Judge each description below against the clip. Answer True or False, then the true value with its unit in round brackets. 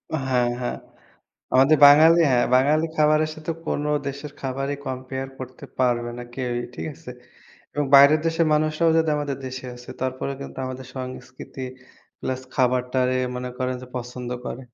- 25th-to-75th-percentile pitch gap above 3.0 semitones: False (2.7 semitones)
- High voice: False (130 Hz)